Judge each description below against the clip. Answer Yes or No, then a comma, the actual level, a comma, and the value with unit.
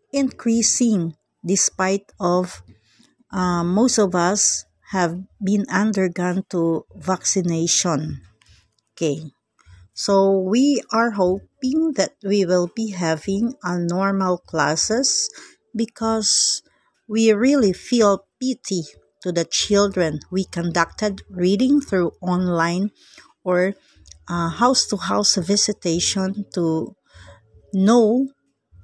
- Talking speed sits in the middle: No, slow, 95 wpm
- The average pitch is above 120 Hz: Yes, high, 190 Hz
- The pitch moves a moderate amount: Yes, average, 4.2 semitones